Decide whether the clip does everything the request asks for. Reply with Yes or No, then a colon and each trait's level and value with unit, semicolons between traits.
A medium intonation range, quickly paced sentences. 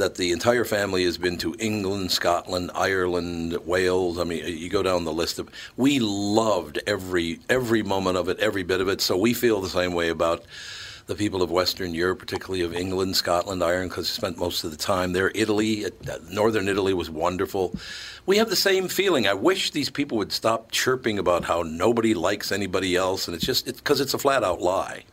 Yes: average, 3.8 semitones; fast, 210 wpm